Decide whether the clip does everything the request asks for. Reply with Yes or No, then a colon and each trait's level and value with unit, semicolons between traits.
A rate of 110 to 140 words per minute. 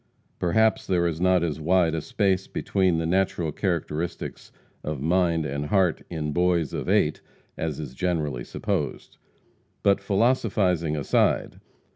Yes: slow, 135 wpm